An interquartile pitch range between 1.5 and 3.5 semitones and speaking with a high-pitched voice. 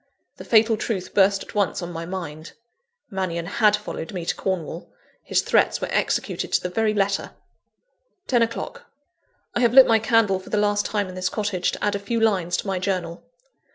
Yes: average, 2.9 semitones; high, 195 Hz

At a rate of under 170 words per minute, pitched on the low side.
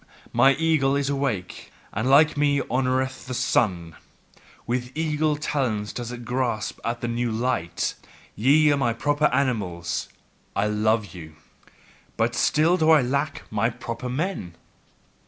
Yes: average, 140 wpm; low, 125 Hz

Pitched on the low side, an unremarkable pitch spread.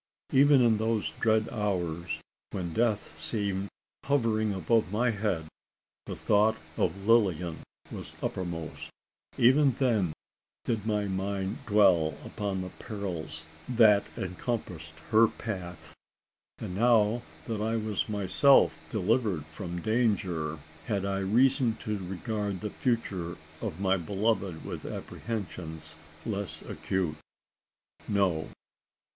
Yes: low, 100 Hz; average, 3.8 semitones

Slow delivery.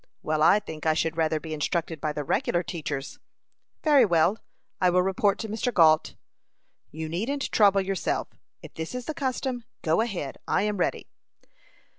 No: average, 170 wpm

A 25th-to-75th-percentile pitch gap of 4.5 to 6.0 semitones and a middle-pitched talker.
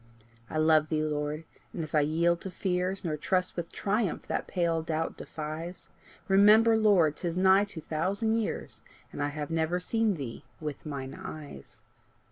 No: average, 3.7 semitones; medium, 165 Hz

